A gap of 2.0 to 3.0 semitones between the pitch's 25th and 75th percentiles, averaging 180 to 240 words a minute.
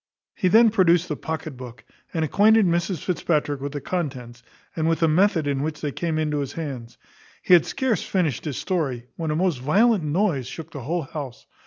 No: average, 4.2 semitones; average, 200 wpm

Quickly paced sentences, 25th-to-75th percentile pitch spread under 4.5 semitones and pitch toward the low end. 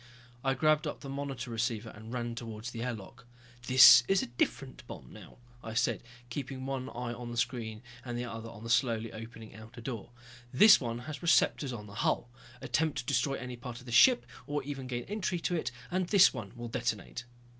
Yes: fast, 210 wpm; average, 2.9 semitones; low, 120 Hz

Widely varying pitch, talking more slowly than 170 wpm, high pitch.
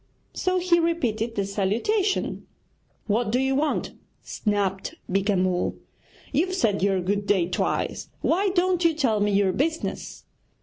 Yes: wide, 9.0 semitones; average, 140 wpm; high, 225 Hz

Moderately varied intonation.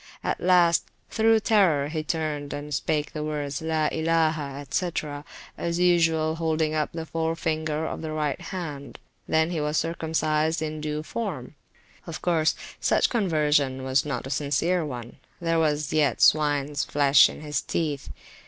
No: narrow, 1.8 semitones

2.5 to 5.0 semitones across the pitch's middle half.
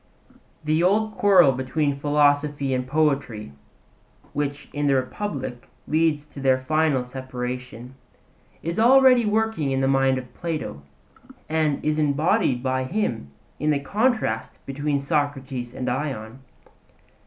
Yes: average, 3.2 semitones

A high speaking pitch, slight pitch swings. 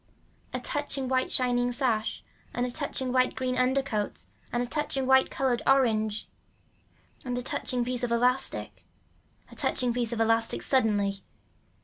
Yes: very high, 250 Hz; narrow, 1.9 semitones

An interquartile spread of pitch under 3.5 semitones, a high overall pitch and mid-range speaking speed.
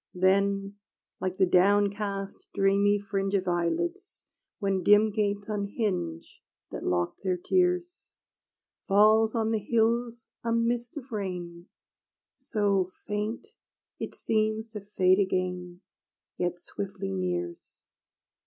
No: average, 3.0 semitones; high, 200 Hz; slow, 110 wpm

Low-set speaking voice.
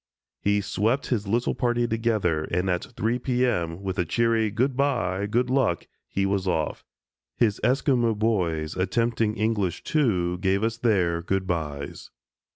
Yes: low, 105 Hz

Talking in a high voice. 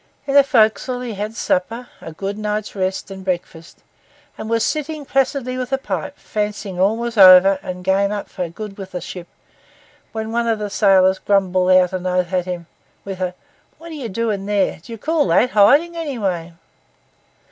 Yes: high, 205 Hz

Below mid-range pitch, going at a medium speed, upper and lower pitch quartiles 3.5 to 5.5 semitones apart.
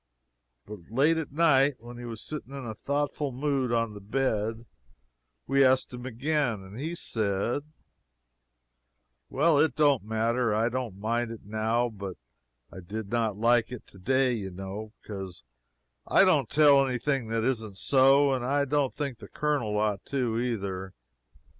Yes: low, 120 Hz; average, 160 wpm; average, 4.1 semitones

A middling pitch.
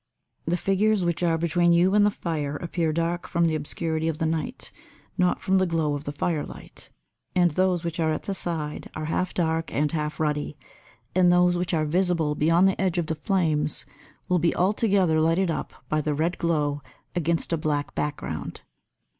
Yes: medium, 165 Hz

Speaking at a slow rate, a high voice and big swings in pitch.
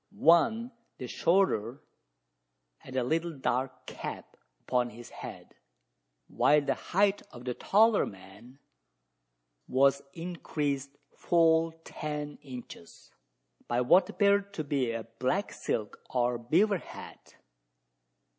No: slow, 110 wpm; medium, 145 Hz; wide, 5.7 semitones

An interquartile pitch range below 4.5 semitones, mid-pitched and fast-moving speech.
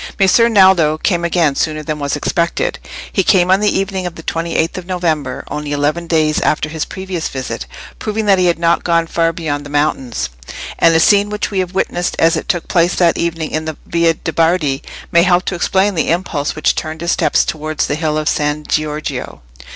Yes: average, 2.9 semitones; medium, 165 Hz; fast, 215 wpm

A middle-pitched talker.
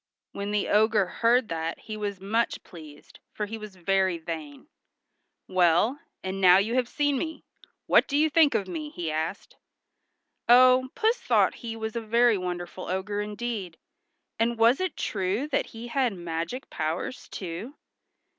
No: high, 210 Hz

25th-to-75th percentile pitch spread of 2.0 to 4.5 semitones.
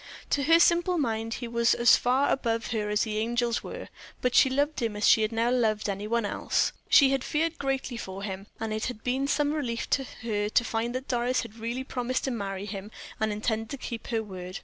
Yes: average, 3.4 semitones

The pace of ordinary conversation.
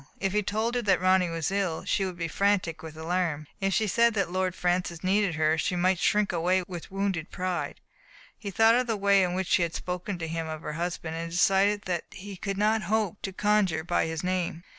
No: fast, 225 wpm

